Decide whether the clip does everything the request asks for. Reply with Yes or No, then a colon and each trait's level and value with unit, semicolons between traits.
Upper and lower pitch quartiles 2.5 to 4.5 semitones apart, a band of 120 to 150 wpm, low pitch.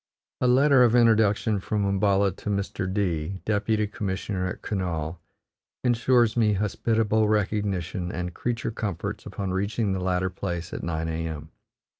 Yes: average, 3.1 semitones; average, 140 wpm; low, 100 Hz